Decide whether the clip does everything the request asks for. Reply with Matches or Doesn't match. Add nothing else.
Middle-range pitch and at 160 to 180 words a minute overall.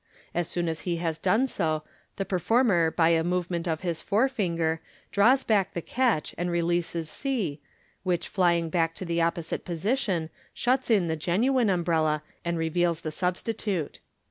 Matches